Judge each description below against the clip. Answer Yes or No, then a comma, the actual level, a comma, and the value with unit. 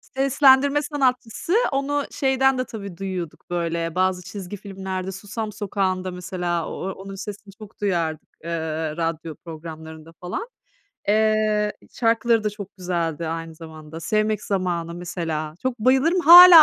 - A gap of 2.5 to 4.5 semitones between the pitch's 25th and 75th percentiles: No, average, 5.1 semitones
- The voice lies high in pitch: Yes, high, 195 Hz